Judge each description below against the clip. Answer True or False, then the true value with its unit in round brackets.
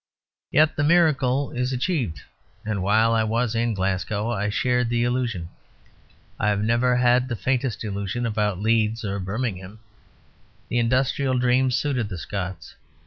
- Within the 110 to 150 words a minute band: True (145 wpm)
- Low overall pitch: True (115 Hz)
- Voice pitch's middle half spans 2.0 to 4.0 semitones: True (3.5 semitones)